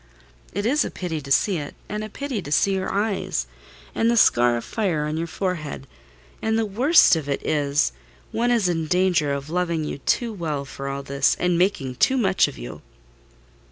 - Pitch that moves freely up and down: Yes, wide, 6.4 semitones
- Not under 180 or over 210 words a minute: Yes, average, 195 wpm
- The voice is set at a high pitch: No, medium, 170 Hz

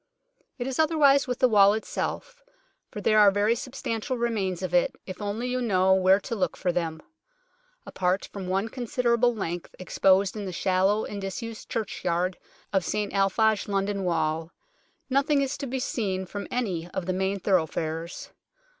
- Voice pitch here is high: Yes, high, 200 Hz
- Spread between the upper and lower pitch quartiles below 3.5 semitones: No, average, 4.2 semitones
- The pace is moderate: Yes, average, 165 wpm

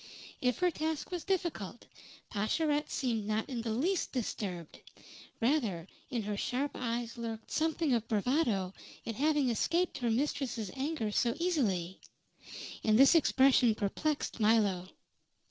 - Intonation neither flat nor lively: No, wide, 5.7 semitones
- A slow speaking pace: Yes, slow, 130 wpm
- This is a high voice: Yes, high, 240 Hz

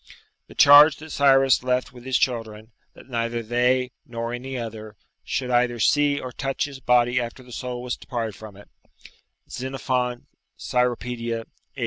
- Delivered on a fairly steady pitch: Yes, narrow, 2.0 semitones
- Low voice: Yes, low, 125 Hz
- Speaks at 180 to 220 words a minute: No, average, 155 wpm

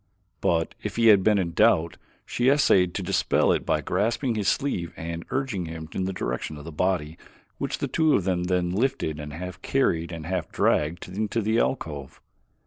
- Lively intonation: No, average, 4.7 semitones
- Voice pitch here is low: Yes, very low, 90 Hz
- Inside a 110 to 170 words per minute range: No, average, 195 wpm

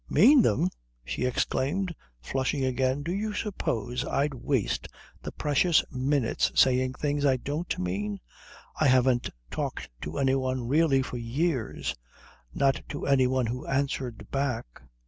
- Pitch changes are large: No, average, 2.8 semitones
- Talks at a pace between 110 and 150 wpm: Yes, average, 140 wpm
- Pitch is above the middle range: No, low, 130 Hz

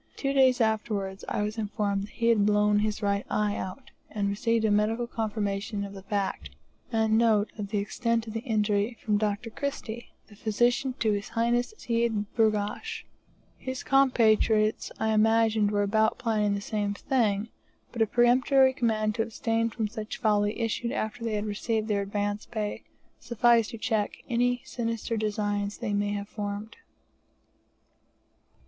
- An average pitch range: No, narrow, 2.0 semitones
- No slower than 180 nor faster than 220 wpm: No, average, 160 wpm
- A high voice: Yes, high, 220 Hz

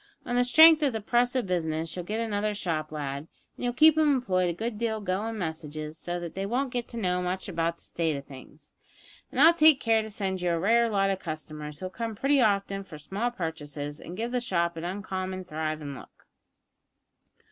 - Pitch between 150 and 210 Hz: Yes, high, 190 Hz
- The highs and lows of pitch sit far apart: Yes, wide, 6.1 semitones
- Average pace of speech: No, fast, 215 wpm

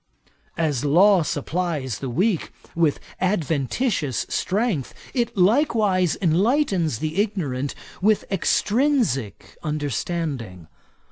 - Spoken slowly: Yes, slow, 85 wpm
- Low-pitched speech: No, medium, 170 Hz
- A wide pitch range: Yes, wide, 6.4 semitones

